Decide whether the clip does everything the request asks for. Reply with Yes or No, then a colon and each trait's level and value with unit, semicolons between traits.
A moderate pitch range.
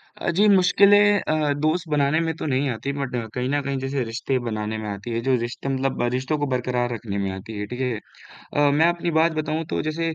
Yes: average, 4.5 semitones